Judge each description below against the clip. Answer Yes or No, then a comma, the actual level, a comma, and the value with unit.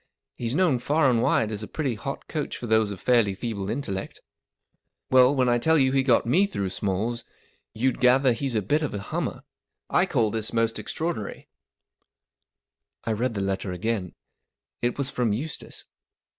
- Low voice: Yes, low, 120 Hz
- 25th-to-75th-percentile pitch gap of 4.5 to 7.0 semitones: No, average, 4.1 semitones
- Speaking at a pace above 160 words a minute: Yes, average, 180 wpm